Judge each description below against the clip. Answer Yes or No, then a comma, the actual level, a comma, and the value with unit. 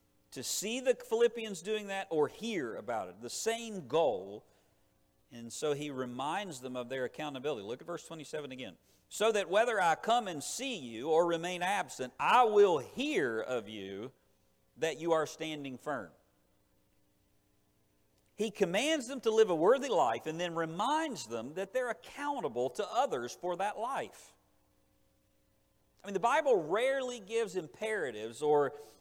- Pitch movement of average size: No, wide, 8.1 semitones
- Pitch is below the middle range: No, high, 190 Hz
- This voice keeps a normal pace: Yes, average, 155 wpm